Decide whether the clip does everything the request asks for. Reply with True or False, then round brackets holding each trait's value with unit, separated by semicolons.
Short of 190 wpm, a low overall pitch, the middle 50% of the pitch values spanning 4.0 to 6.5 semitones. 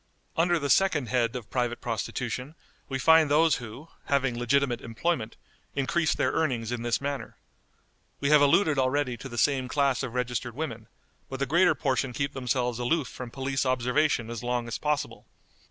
False (170 wpm; 130 Hz; 3.0 semitones)